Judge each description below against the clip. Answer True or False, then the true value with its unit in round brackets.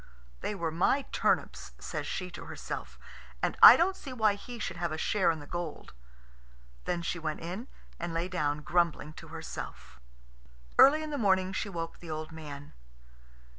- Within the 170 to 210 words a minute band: True (175 wpm)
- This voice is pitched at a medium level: True (175 Hz)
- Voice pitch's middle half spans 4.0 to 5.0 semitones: True (4.3 semitones)